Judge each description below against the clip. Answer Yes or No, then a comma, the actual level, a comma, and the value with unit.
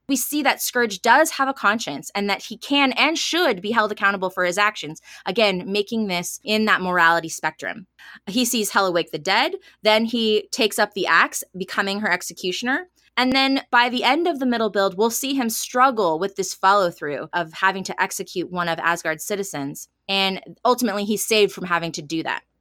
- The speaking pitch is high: Yes, high, 205 Hz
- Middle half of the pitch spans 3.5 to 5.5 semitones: Yes, average, 4.8 semitones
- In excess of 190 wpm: Yes, average, 200 wpm